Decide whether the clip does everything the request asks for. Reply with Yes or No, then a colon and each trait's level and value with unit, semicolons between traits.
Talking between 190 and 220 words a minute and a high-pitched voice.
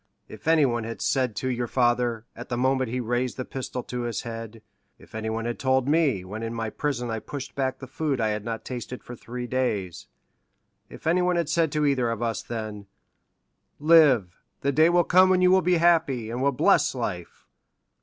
No: average, 195 wpm; low, 125 Hz